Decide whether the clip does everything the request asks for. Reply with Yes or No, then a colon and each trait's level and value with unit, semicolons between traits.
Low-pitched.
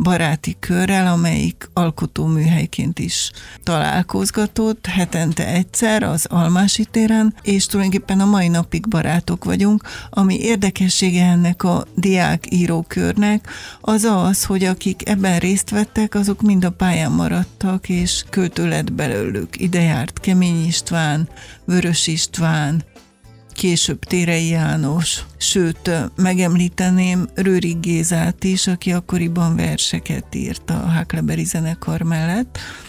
No: medium, 180 Hz